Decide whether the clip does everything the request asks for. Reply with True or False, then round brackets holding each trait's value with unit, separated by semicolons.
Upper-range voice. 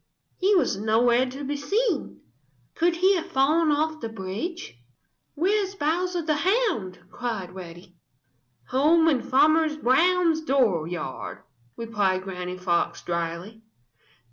True (270 Hz)